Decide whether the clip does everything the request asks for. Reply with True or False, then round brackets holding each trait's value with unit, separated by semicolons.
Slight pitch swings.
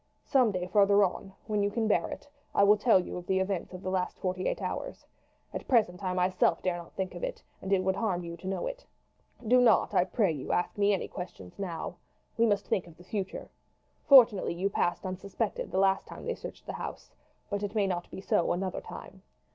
True (2.2 semitones)